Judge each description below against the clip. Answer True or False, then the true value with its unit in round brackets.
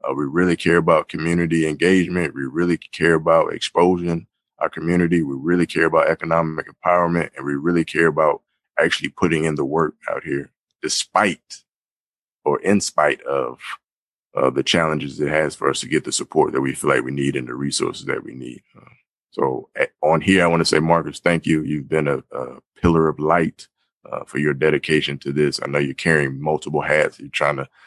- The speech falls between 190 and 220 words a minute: True (200 wpm)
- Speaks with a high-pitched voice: False (80 Hz)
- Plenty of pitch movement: False (2.9 semitones)